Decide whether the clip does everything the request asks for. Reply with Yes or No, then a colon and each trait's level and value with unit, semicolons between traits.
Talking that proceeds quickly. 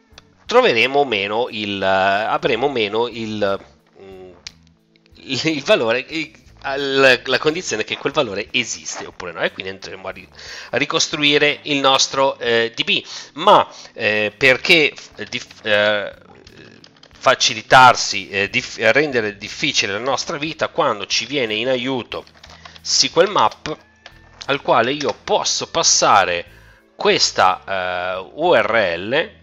No: average, 120 wpm